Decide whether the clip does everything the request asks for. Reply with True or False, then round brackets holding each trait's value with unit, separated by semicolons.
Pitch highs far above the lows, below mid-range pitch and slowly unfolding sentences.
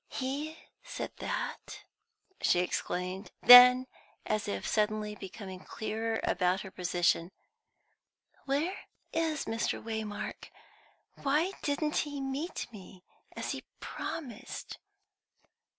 False (6.5 semitones; 225 Hz; 100 wpm)